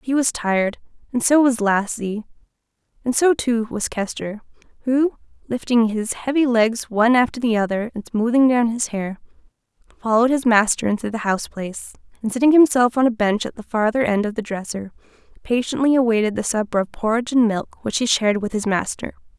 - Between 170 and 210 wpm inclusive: Yes, average, 185 wpm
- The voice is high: Yes, high, 230 Hz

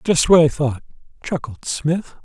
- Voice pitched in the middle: Yes, medium, 150 Hz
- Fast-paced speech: No, average, 160 wpm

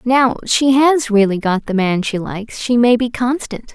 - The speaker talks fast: Yes, fast, 210 wpm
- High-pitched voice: Yes, high, 235 Hz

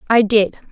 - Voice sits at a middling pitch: No, high, 215 Hz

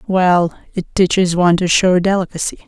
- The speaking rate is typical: Yes, average, 155 wpm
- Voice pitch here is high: No, medium, 180 Hz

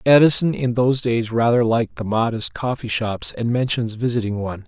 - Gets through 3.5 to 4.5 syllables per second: No, 5.5 syllables/s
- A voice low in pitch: Yes, low, 120 Hz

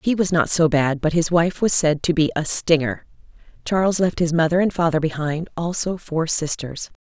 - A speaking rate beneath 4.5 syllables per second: No, 5.0 syllables/s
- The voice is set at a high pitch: No, medium, 165 Hz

